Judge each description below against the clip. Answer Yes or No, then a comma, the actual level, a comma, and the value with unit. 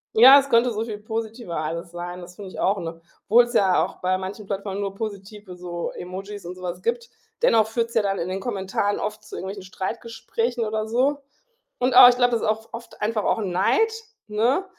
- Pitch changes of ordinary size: Yes, average, 3.7 semitones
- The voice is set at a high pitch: Yes, high, 210 Hz